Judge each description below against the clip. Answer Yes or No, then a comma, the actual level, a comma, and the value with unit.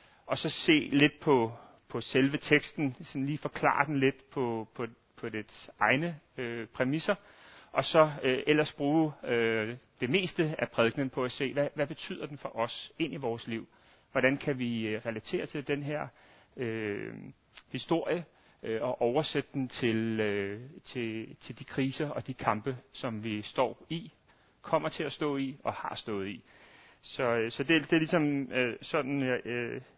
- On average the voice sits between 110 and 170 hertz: Yes, low, 135 Hz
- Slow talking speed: No, average, 180 wpm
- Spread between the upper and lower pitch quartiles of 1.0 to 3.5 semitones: No, average, 4.4 semitones